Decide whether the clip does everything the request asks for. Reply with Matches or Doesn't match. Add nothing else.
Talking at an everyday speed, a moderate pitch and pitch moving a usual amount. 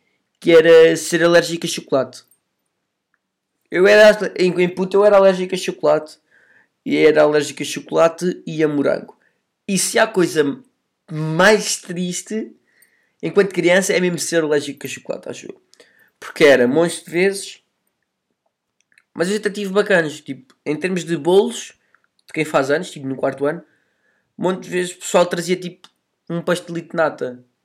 Matches